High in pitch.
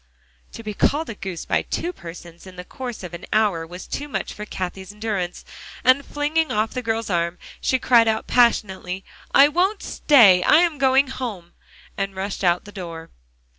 Yes: high, 210 Hz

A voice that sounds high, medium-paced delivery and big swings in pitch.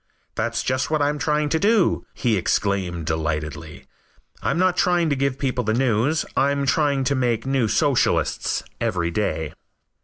No: low, 130 Hz; average, 160 wpm; wide, 6.1 semitones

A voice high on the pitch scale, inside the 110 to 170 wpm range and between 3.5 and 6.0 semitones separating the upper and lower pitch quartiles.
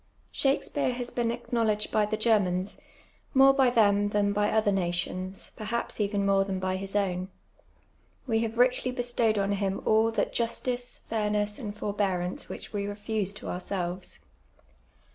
No: high, 210 Hz; average, 150 wpm; average, 2.9 semitones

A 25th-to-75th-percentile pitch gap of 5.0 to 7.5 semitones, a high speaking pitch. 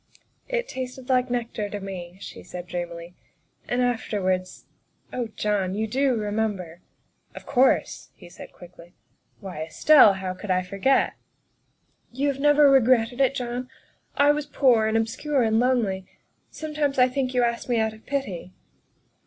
Yes: wide, 5.4 semitones; high, 230 Hz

